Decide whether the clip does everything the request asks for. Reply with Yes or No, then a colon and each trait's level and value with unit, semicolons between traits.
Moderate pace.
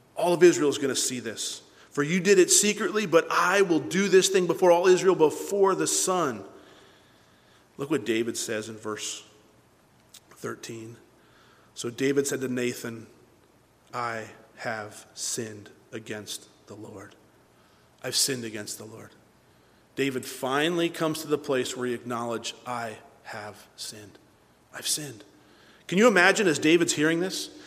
Yes: average, 150 wpm